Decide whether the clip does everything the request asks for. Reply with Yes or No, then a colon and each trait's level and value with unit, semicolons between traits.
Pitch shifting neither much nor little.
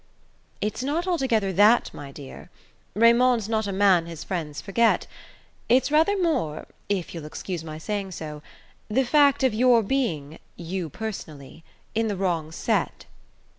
No: wide, 7.0 semitones